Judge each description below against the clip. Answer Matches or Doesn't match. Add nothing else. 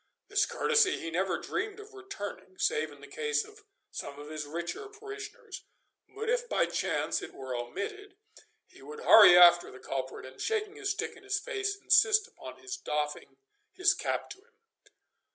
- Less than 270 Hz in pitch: Doesn't match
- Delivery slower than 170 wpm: Doesn't match